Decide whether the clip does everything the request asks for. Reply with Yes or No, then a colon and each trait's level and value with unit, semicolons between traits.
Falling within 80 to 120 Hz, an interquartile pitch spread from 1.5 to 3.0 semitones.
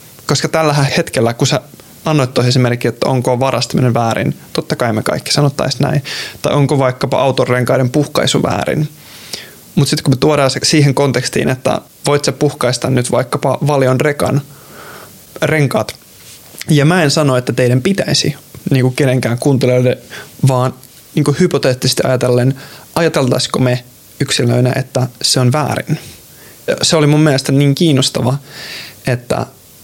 No: low, 135 Hz; average, 2.7 semitones